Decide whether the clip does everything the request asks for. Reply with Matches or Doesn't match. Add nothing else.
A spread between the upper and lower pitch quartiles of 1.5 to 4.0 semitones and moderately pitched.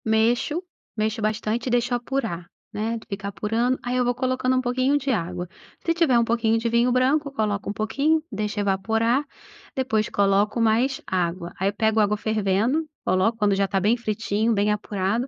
Doesn't match